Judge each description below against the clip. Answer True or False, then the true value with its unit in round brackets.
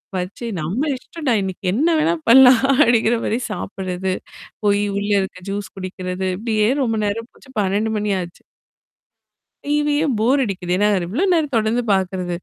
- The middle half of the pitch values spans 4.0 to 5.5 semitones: True (4.8 semitones)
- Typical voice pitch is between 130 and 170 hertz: False (210 Hz)